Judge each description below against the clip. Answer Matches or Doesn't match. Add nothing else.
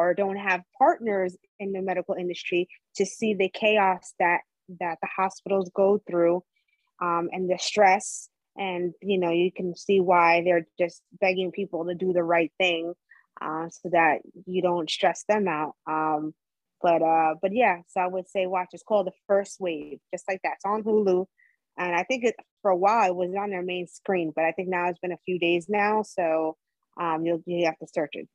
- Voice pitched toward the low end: Doesn't match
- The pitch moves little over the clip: Matches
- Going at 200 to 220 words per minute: Matches